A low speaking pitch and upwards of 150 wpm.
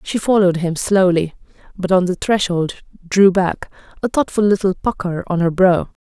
No: medium, 185 Hz; average, 165 wpm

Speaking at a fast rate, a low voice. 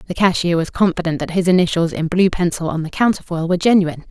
No: fast, 220 wpm; medium, 175 Hz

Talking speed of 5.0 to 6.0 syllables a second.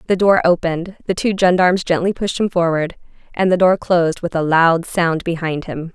Yes: 5.4 syllables/s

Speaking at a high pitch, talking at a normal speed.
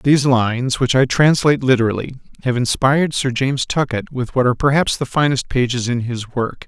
No: low, 130 Hz; average, 190 wpm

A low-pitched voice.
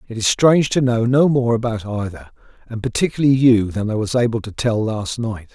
Yes: low, 115 Hz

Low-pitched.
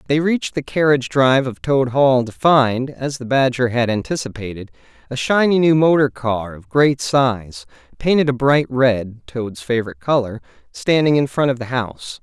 Yes: low, 130 Hz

